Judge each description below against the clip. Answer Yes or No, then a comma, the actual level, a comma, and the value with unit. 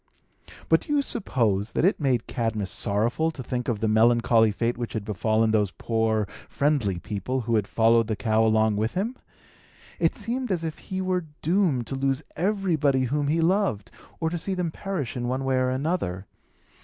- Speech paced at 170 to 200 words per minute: Yes, average, 190 wpm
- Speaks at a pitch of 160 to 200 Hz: No, low, 125 Hz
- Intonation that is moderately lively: No, wide, 6.7 semitones